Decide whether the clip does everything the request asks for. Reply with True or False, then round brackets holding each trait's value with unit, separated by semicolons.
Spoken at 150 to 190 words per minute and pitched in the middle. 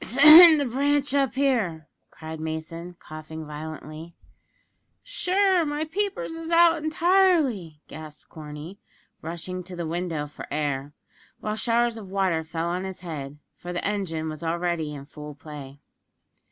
False (140 wpm; 175 Hz)